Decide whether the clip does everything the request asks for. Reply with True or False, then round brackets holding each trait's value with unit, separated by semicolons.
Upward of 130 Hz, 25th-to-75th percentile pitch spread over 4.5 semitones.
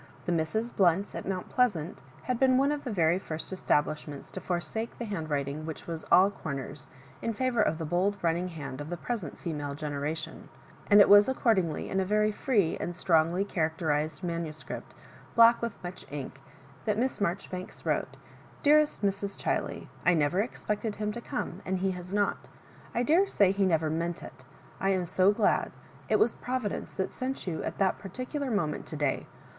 True (185 Hz; 4.9 semitones)